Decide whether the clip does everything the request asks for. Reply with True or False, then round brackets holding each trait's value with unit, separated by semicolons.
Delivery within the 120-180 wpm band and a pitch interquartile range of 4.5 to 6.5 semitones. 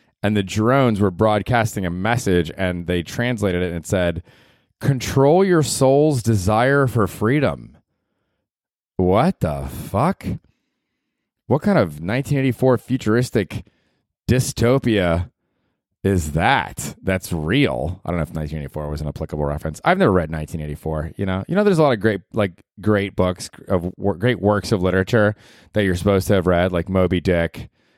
True (155 wpm; 5.2 semitones)